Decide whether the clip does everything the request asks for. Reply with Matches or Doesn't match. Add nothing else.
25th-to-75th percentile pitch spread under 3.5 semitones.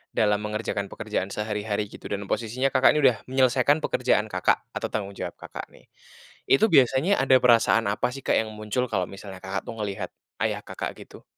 Doesn't match